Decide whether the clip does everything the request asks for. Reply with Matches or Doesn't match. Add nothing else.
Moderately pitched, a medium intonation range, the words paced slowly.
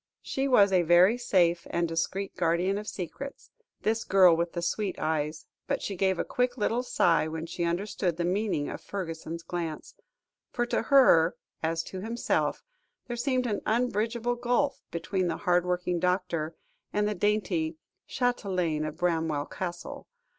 Doesn't match